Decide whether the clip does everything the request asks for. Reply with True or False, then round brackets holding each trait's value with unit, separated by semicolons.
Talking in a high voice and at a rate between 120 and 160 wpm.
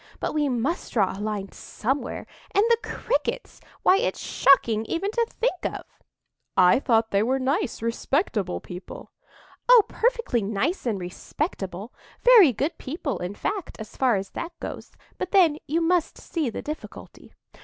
True (270 Hz; 150 wpm)